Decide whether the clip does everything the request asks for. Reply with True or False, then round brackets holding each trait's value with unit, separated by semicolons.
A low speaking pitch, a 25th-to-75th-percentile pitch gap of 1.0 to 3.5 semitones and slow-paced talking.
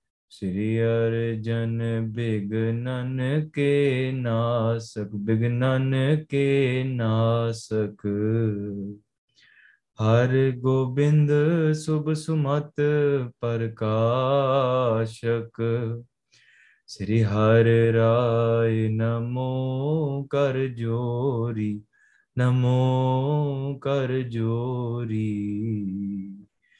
True (115 Hz; 2.8 semitones; 50 wpm)